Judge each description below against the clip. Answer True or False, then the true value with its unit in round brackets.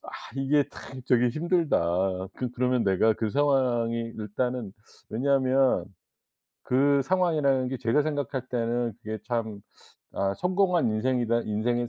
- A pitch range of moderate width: True (3.4 semitones)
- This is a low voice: True (125 Hz)